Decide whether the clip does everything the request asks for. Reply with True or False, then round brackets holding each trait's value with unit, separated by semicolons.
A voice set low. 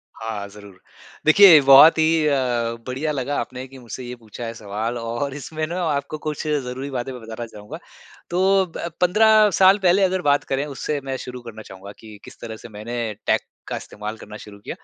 True (130 Hz)